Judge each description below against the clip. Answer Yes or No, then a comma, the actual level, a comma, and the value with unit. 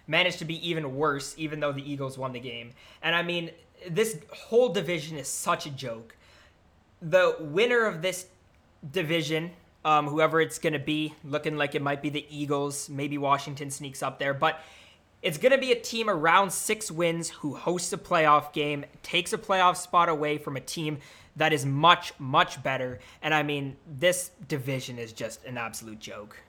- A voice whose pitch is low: No, medium, 155 Hz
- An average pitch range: Yes, average, 3.6 semitones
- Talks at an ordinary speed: Yes, average, 190 wpm